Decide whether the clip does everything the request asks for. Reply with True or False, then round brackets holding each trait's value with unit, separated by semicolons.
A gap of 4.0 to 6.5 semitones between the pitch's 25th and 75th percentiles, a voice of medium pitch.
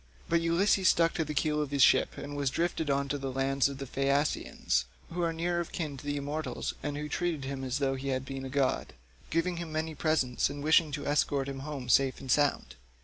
False (2.7 semitones; 145 Hz)